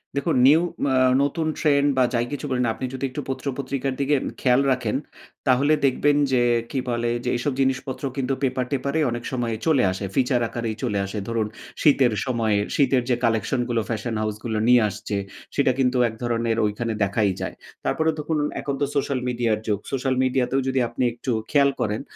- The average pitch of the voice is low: Yes, low, 125 Hz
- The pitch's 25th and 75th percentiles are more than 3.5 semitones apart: No, average, 2.8 semitones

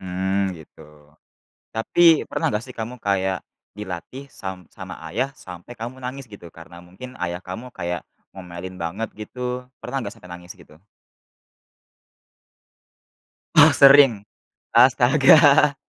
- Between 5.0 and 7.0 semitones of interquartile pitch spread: Yes, wide, 5.6 semitones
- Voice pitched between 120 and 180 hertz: No, low, 100 Hz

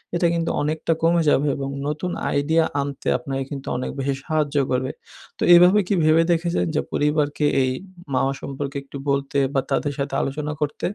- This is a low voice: No, medium, 145 Hz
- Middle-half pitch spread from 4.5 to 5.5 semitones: No, narrow, 2.6 semitones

